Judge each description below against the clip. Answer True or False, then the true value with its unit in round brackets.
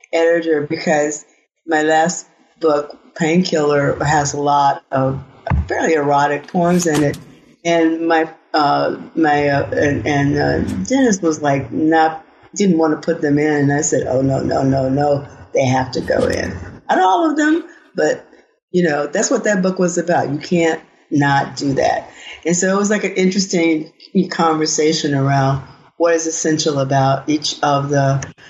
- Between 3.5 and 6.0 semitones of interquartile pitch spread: False (2.8 semitones)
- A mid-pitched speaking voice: True (155 Hz)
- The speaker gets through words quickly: False (170 wpm)